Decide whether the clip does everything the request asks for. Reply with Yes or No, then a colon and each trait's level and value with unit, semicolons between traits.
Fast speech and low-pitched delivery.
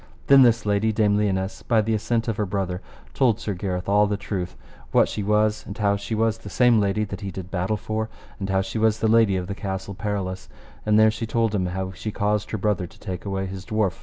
Yes: fast, 240 wpm; low, 105 Hz